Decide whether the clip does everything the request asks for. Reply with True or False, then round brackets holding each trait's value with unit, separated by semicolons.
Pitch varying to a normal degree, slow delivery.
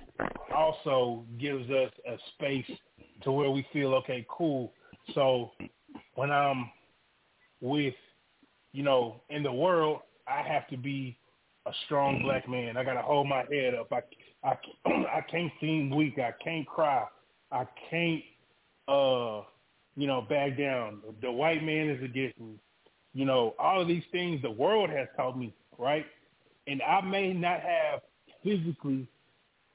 False (3.2 semitones; 150 wpm)